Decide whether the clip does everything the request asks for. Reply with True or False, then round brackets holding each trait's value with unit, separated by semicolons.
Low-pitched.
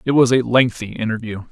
True (120 Hz)